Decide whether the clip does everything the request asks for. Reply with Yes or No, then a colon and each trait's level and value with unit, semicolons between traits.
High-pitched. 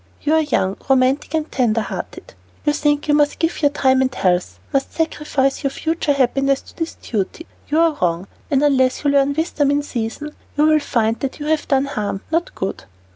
Yes: very high, 280 Hz